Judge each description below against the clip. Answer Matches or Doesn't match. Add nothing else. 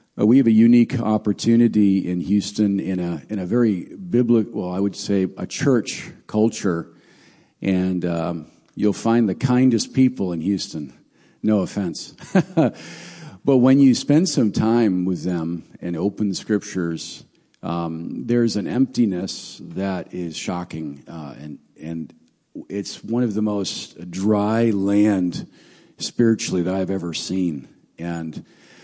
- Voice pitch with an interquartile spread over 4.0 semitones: Matches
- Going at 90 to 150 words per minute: Matches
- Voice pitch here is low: Matches